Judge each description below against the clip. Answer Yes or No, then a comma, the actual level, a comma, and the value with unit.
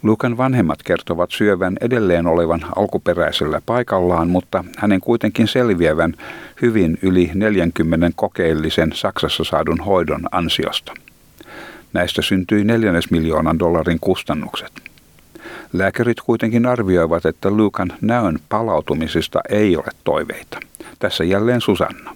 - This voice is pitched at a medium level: No, very low, 95 Hz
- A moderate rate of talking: Yes, average, 105 wpm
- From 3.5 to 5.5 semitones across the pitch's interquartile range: Yes, average, 4.5 semitones